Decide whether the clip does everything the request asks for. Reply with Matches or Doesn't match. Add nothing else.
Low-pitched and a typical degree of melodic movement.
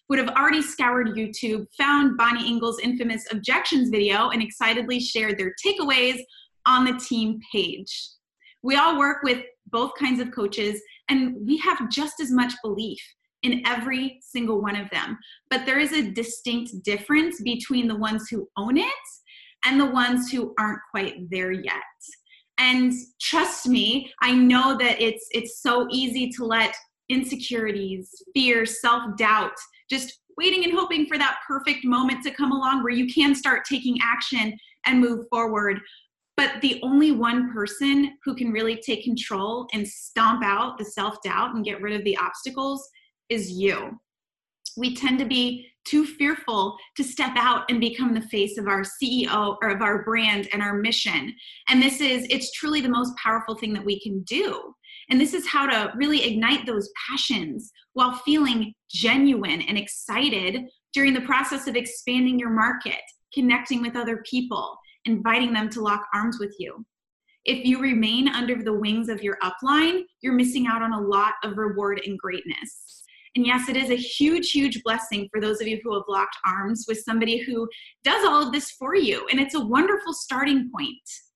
Doesn't match